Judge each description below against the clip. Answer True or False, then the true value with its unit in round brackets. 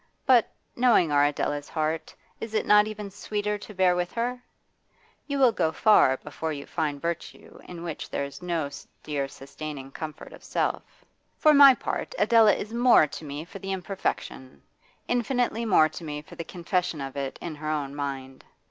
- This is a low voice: False (170 Hz)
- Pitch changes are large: True (6.4 semitones)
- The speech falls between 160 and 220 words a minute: True (180 wpm)